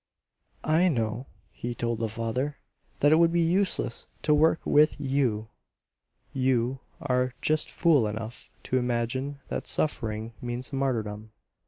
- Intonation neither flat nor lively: Yes, average, 4.3 semitones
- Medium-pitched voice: No, low, 130 Hz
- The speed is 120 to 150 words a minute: Yes, slow, 135 wpm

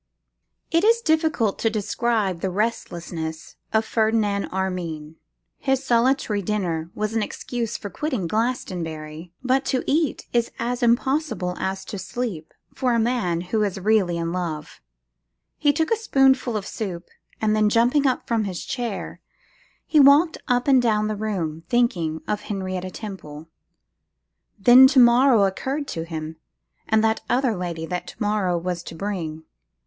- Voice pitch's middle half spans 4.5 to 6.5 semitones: Yes, wide, 5.6 semitones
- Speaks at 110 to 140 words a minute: No, average, 155 wpm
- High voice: Yes, high, 215 Hz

